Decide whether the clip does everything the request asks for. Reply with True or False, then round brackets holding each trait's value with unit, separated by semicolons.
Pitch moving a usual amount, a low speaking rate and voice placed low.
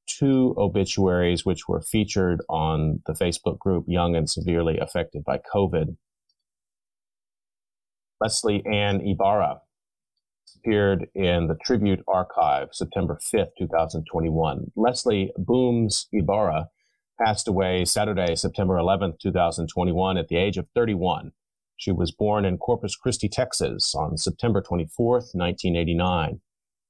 True (3.3 semitones; 115 wpm; 95 Hz)